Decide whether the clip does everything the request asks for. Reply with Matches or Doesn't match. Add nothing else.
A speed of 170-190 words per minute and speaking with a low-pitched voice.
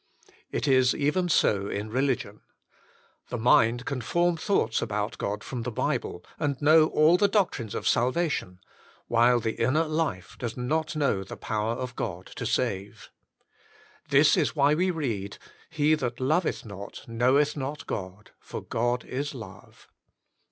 Doesn't match